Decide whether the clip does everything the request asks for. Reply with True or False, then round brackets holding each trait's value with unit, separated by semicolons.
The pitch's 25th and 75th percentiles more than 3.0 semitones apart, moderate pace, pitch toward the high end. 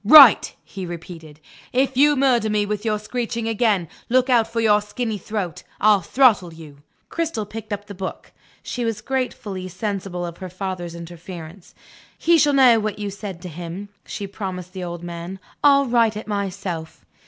True (4.4 semitones; 175 wpm; 205 Hz)